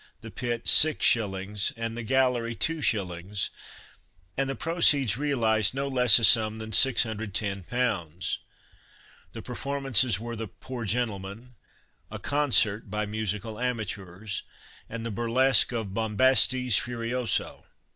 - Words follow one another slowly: Yes, slow, 115 wpm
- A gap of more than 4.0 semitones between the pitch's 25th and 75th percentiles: No, average, 3.3 semitones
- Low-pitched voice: Yes, low, 115 Hz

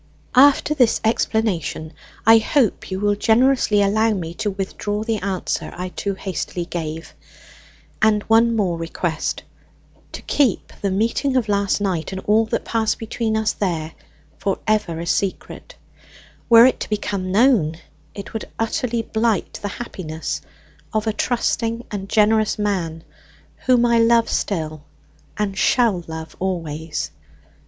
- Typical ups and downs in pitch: Yes, average, 3.7 semitones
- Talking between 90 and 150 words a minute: Yes, average, 140 wpm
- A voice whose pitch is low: No, high, 205 Hz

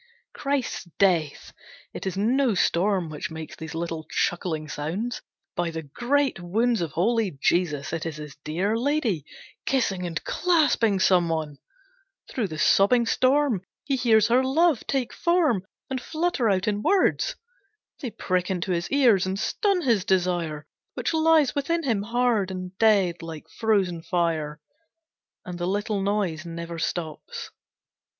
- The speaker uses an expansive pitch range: Yes, wide, 6.5 semitones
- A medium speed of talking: Yes, average, 145 wpm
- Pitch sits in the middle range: No, high, 195 Hz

